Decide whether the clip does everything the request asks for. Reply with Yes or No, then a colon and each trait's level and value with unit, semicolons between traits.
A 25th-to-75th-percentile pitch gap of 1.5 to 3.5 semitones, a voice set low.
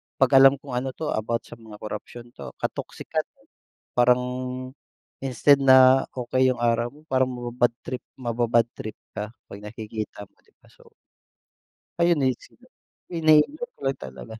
Yes: narrow, 2.6 semitones; low, 125 Hz